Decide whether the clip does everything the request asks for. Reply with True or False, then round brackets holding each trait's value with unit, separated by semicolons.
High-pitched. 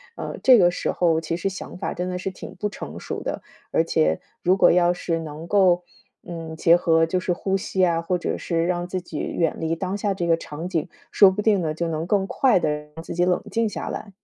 False (175 Hz)